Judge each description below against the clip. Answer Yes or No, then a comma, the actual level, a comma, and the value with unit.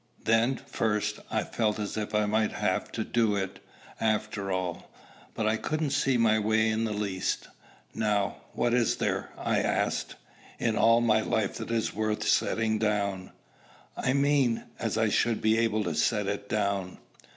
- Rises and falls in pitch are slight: Yes, narrow, 1.6 semitones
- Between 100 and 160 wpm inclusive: No, average, 170 wpm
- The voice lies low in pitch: Yes, low, 110 Hz